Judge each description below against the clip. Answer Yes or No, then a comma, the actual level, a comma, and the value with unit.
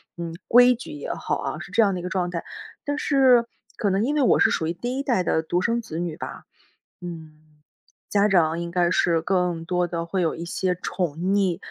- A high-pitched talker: No, medium, 180 Hz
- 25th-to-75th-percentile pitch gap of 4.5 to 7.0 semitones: Yes, average, 4.9 semitones